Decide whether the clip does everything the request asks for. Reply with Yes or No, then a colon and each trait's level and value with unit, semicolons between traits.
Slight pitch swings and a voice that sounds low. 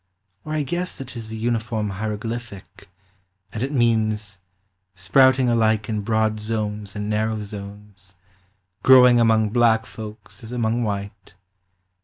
Yes: narrow, 2.2 semitones; low, 110 Hz